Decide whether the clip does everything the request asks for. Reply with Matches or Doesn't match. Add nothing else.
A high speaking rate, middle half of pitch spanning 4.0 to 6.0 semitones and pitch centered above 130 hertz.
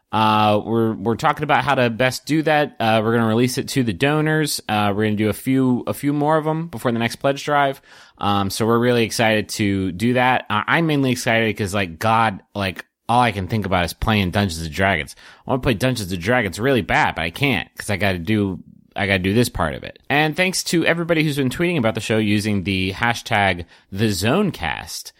Doesn't match